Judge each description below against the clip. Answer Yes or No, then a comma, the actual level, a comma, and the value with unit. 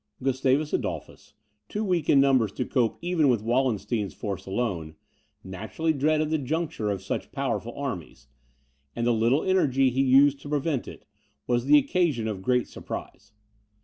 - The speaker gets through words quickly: No, average, 155 wpm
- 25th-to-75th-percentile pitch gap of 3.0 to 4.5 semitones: No, average, 5.0 semitones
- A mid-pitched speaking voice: No, low, 130 Hz